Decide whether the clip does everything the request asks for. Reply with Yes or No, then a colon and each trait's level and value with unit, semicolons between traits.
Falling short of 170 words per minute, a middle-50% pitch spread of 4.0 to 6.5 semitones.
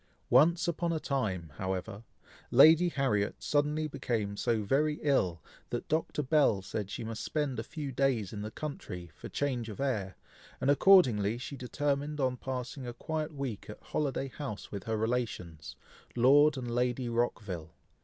Yes: average, 160 wpm; wide, 5.5 semitones